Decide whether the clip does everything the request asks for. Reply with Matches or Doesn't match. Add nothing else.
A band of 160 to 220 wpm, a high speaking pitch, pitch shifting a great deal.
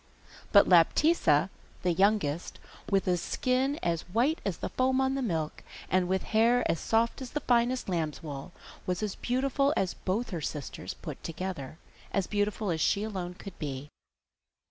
Matches